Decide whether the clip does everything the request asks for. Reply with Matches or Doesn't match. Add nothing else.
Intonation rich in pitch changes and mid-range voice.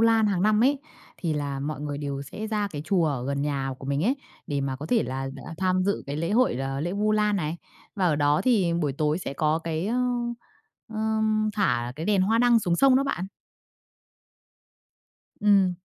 Matches